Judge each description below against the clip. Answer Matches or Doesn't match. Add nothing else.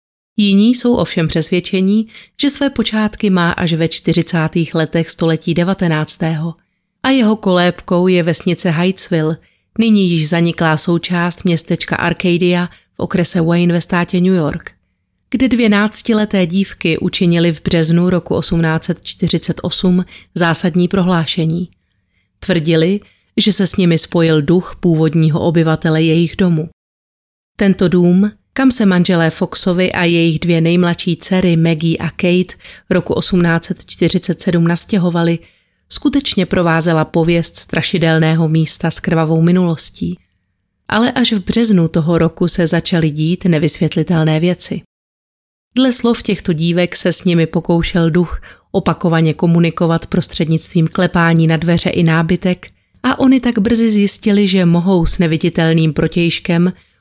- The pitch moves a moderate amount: Doesn't match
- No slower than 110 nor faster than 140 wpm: Matches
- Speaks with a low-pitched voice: Doesn't match